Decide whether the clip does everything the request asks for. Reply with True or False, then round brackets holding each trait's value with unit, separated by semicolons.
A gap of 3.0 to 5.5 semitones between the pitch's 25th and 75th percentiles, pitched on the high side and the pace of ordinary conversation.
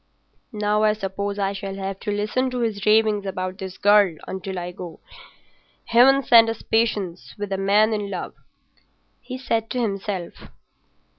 False (2.5 semitones; 205 Hz; 160 wpm)